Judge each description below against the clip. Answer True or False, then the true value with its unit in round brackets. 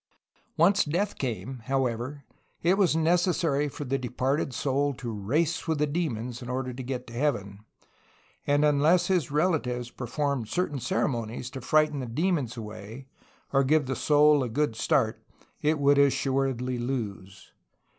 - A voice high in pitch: False (135 Hz)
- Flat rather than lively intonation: False (3.7 semitones)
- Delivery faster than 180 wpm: False (155 wpm)